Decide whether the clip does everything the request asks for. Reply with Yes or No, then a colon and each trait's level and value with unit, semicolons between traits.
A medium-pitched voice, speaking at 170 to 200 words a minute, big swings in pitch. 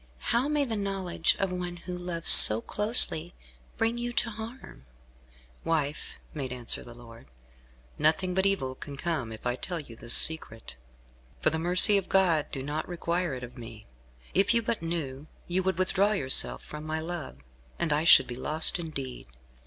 Yes: medium, 165 Hz; average, 175 wpm; wide, 5.9 semitones